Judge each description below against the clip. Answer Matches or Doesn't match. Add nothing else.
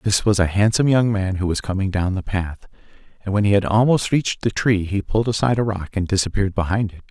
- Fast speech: Matches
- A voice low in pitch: Matches